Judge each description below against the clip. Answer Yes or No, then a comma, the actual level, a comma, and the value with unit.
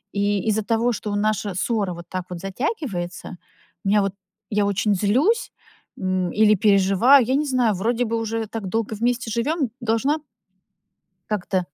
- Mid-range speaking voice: No, high, 215 Hz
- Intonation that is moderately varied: Yes, average, 3.3 semitones